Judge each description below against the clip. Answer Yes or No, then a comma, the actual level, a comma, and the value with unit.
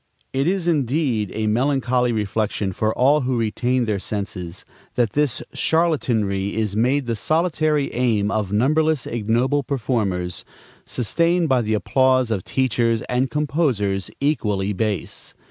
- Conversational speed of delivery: No, slow, 130 wpm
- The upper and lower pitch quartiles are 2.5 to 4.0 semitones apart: No, average, 4.9 semitones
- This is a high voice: No, low, 120 Hz